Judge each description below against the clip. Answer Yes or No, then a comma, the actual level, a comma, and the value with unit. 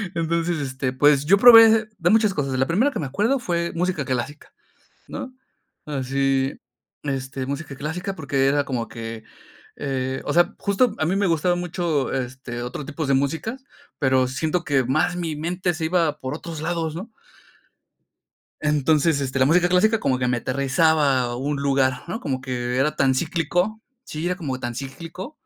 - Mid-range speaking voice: Yes, medium, 150 Hz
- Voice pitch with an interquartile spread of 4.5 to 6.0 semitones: Yes, average, 4.8 semitones